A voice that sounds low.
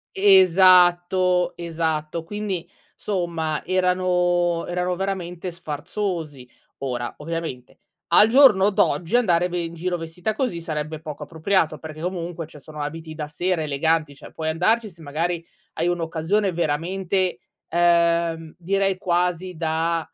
No: medium, 170 Hz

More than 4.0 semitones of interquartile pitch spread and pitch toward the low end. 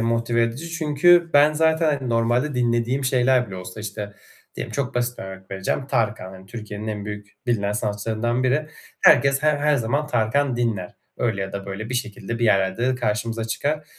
Yes: average, 4.7 semitones; low, 120 Hz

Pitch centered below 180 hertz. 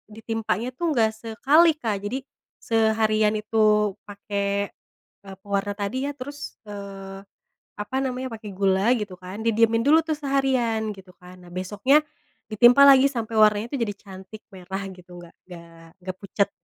No: high, 215 Hz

